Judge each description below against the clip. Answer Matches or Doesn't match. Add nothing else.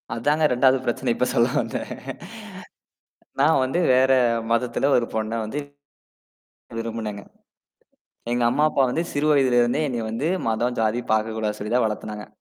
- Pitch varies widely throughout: Doesn't match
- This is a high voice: Doesn't match